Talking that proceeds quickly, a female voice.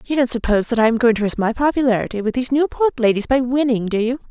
Yes: fast, 265 wpm; female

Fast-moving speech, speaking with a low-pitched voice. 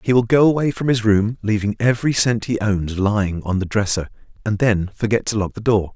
Yes: fast, 220 wpm; low, 110 Hz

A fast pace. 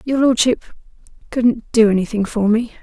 No: average, 150 wpm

